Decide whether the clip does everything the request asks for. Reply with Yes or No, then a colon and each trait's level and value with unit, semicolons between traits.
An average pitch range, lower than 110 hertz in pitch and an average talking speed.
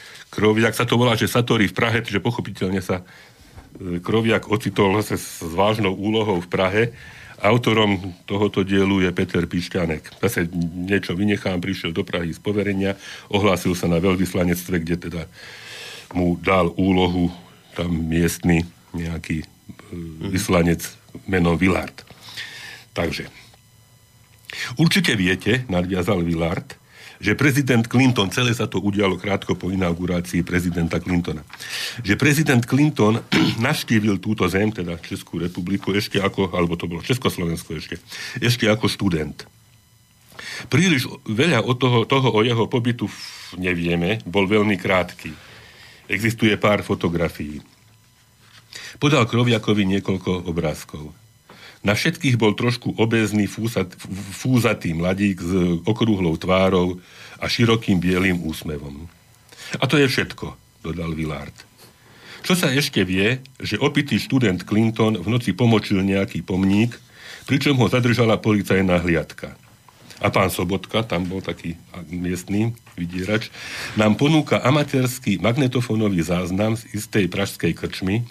Yes: average, 4.3 semitones; low, 100 Hz; average, 120 wpm